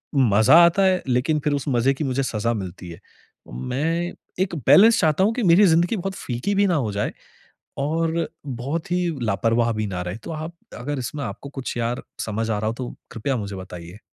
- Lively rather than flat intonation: Yes, wide, 7.1 semitones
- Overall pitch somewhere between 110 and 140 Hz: Yes, low, 135 Hz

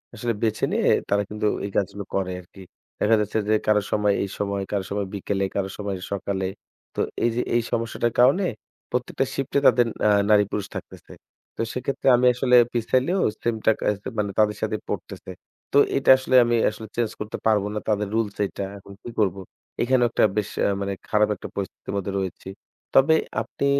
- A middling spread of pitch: Yes, average, 3.0 semitones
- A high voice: No, low, 105 Hz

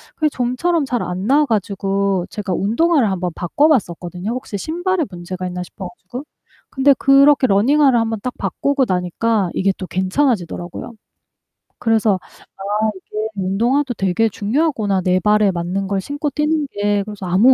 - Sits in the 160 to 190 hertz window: No, high, 210 Hz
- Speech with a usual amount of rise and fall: No, wide, 6.4 semitones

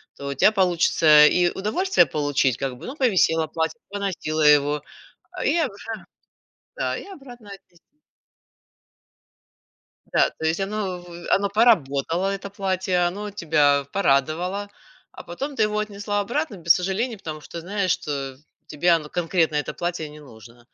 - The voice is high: No, medium, 180 Hz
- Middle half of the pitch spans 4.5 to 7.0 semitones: Yes, average, 5.1 semitones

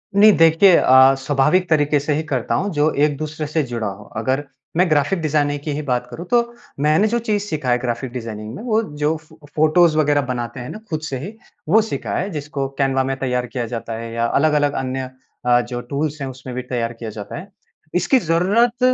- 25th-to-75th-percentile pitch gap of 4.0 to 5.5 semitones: Yes, average, 4.3 semitones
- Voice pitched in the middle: Yes, medium, 145 Hz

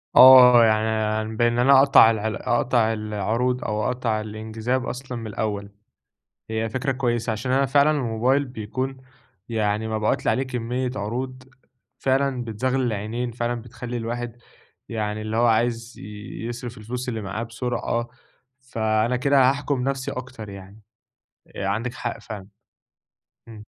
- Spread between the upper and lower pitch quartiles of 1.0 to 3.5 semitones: Yes, narrow, 2.6 semitones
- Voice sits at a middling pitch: No, low, 120 Hz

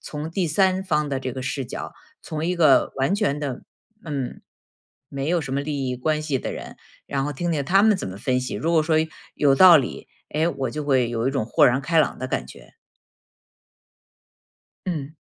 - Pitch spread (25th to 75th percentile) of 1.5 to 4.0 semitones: Yes, average, 3.5 semitones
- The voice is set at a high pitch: No, medium, 145 Hz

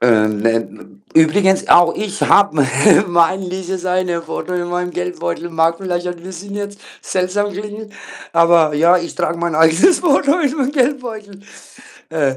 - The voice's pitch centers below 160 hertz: No, medium, 180 Hz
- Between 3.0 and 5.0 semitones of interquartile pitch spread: Yes, average, 4.0 semitones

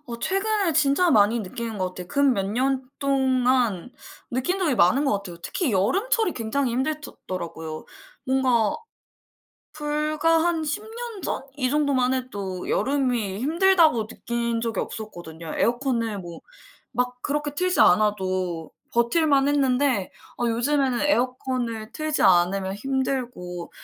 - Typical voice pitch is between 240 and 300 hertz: Yes, very high, 250 Hz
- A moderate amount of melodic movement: No, wide, 5.7 semitones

